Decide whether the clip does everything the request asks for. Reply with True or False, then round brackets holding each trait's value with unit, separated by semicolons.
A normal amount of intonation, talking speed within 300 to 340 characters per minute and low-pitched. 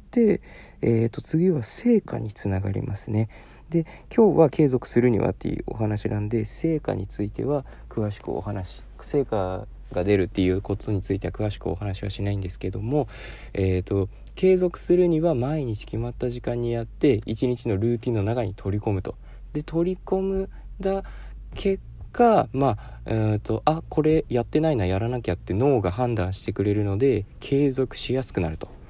False (6.4 semitones; 310 characters per minute; 115 Hz)